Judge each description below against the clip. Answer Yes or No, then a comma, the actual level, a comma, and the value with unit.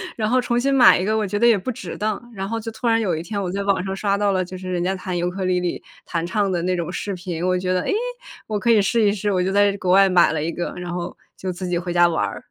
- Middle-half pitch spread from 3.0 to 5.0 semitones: No, narrow, 2.6 semitones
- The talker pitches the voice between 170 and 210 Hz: Yes, high, 190 Hz